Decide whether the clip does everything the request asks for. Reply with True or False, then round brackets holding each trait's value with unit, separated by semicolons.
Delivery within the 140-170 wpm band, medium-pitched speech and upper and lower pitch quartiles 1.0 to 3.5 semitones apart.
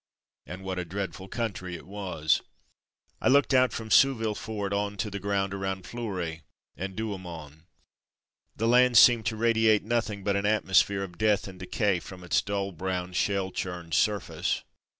False (165 wpm; 100 Hz; 2.9 semitones)